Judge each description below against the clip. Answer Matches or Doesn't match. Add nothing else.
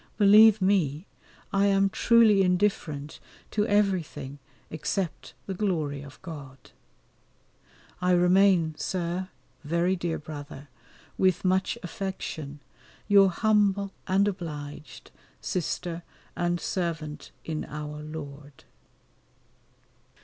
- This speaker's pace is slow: Matches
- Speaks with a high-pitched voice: Doesn't match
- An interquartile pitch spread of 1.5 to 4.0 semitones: Doesn't match